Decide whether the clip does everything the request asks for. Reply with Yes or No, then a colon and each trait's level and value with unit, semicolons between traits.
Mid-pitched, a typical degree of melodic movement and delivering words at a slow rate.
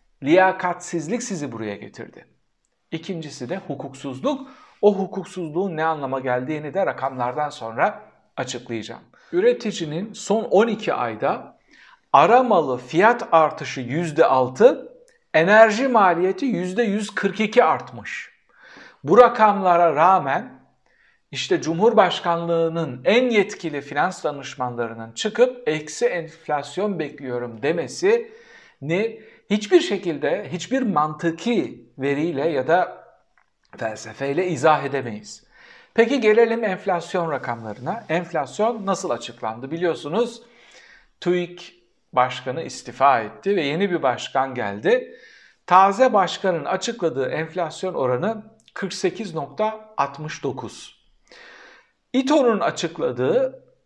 No: medium, 180 Hz; wide, 7.1 semitones; slow, 85 wpm